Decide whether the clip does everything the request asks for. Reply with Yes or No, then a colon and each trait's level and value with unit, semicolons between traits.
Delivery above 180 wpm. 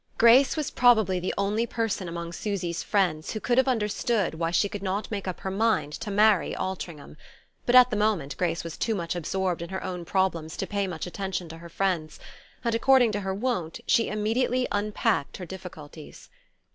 Yes: average, 195 wpm